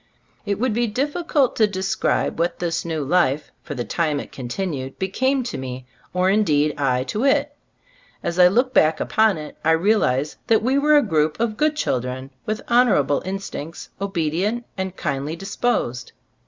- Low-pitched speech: No, medium, 185 Hz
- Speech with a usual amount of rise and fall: No, wide, 7.3 semitones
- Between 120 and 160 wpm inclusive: No, average, 180 wpm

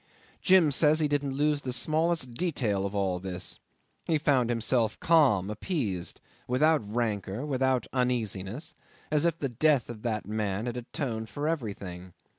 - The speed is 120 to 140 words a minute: No, average, 150 wpm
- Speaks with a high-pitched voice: No, low, 125 Hz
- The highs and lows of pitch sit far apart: Yes, wide, 5.9 semitones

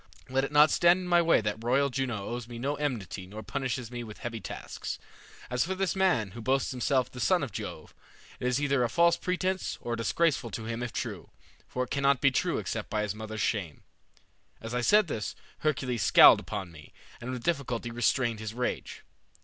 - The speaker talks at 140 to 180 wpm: No, fast, 205 wpm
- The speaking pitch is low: Yes, low, 125 Hz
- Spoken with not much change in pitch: No, average, 3.9 semitones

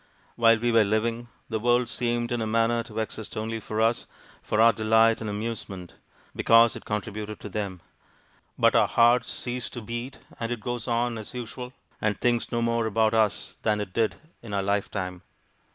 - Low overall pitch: Yes, low, 115 Hz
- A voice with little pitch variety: Yes, narrow, 1.7 semitones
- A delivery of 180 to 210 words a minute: Yes, average, 185 wpm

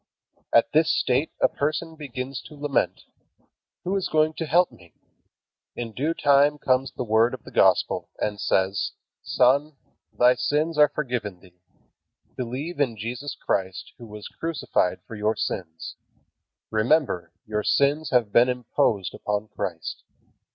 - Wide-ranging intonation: Yes, wide, 5.7 semitones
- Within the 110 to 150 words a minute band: Yes, average, 145 wpm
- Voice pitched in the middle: No, low, 125 Hz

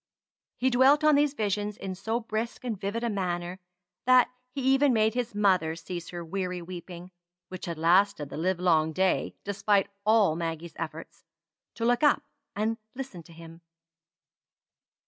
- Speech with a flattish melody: No, average, 5.0 semitones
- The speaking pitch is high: Yes, high, 195 Hz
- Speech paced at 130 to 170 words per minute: Yes, average, 155 wpm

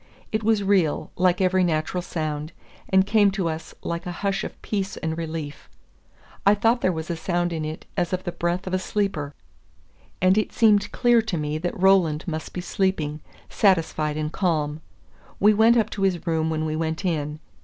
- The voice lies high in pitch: No, medium, 175 Hz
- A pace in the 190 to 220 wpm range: Yes, average, 195 wpm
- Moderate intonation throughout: Yes, average, 3.6 semitones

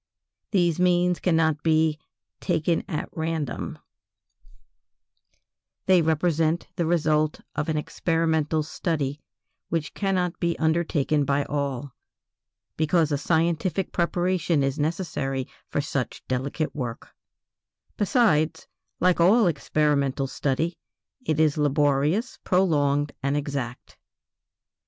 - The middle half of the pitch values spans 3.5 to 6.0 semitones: No, average, 3.0 semitones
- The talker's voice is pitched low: No, medium, 155 Hz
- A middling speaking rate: No, slow, 100 wpm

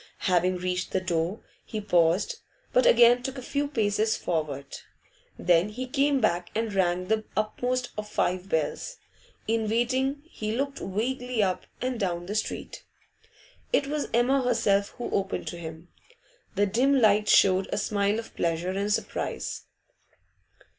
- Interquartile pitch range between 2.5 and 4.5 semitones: No, wide, 5.4 semitones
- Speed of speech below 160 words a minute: Yes, average, 150 wpm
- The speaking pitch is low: No, high, 210 Hz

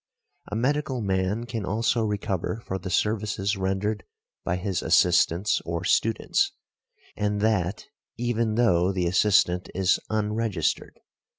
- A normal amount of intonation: Yes, average, 3.0 semitones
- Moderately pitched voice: No, low, 105 Hz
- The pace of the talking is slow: Yes, slow, 120 wpm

